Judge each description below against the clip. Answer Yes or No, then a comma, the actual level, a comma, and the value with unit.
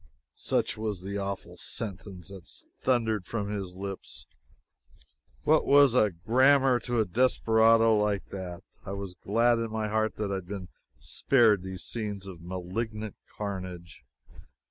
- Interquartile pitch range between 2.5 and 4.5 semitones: Yes, average, 3.1 semitones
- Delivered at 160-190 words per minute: No, average, 140 wpm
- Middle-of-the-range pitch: No, low, 105 Hz